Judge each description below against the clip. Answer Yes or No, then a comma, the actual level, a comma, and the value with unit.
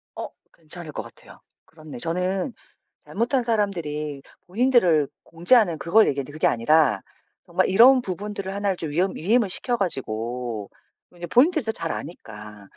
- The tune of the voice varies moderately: No, wide, 6.1 semitones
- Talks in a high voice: No, medium, 175 Hz